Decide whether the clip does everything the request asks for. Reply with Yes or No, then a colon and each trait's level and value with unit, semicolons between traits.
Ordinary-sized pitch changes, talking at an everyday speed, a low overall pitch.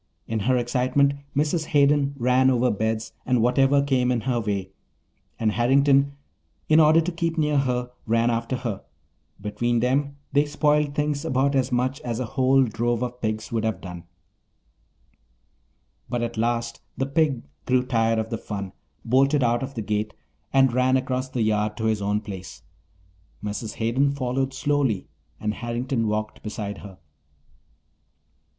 Yes: average, 3.6 semitones; average, 155 wpm; low, 125 Hz